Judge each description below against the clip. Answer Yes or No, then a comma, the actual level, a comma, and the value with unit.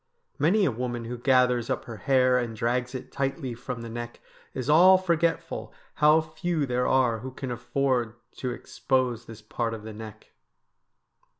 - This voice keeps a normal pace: Yes, average, 170 wpm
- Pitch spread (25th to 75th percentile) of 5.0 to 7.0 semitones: No, average, 2.9 semitones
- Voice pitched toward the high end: No, low, 125 Hz